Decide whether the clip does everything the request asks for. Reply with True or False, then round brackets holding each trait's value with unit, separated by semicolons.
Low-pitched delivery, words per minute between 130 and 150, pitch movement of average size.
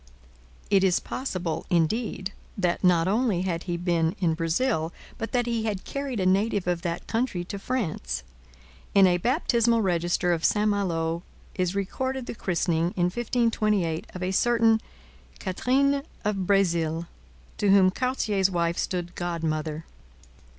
False (185 Hz; 145 wpm; 4.6 semitones)